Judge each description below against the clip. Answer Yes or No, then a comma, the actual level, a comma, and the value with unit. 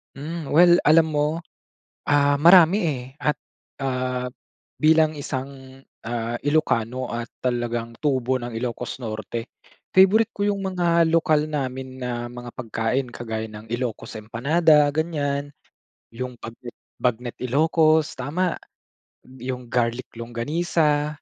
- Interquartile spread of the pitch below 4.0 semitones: No, average, 4.6 semitones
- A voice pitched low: Yes, low, 130 Hz